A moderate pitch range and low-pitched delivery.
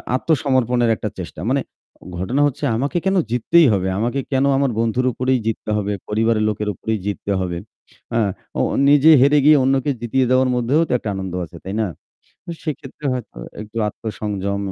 Yes: average, 4.5 semitones; low, 120 Hz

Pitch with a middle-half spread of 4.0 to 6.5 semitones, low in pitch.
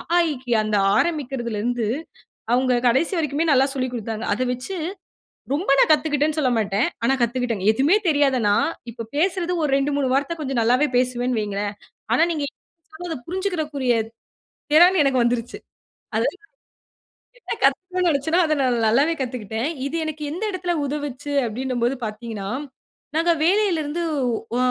No: average, 4.8 semitones; very high, 270 Hz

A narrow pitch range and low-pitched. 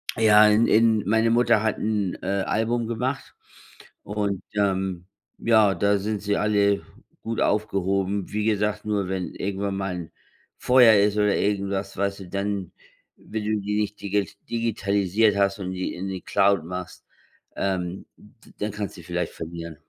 Yes: narrow, 1.8 semitones; low, 100 Hz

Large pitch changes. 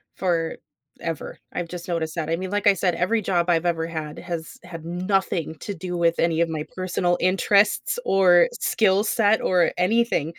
No: narrow, 2.5 semitones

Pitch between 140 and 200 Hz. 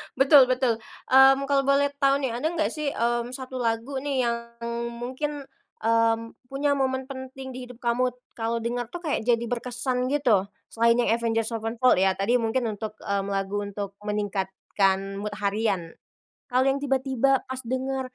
No: high, 245 Hz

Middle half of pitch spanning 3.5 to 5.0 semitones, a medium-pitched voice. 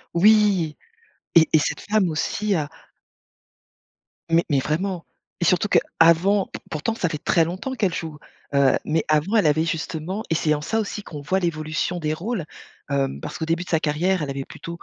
Yes: average, 3.8 semitones; medium, 165 Hz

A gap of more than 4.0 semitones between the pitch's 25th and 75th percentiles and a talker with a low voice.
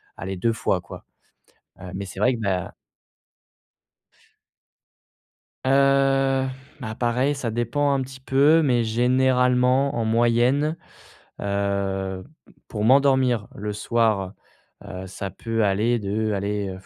Yes: average, 4.8 semitones; low, 115 Hz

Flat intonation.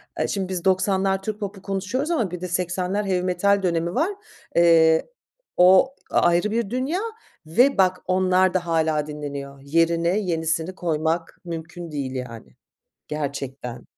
No: average, 3.1 semitones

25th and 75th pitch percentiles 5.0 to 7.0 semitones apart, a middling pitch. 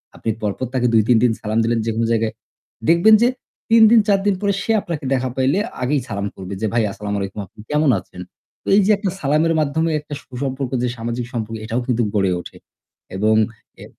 No: wide, 5.6 semitones; low, 125 Hz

